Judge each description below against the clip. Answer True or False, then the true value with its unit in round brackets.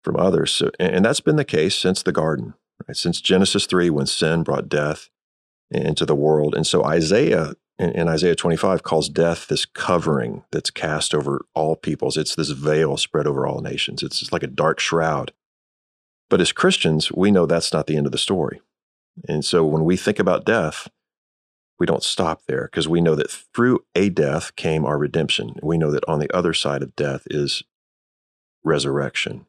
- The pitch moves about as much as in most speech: False (2.1 semitones)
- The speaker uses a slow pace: False (190 wpm)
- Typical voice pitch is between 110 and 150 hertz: False (80 Hz)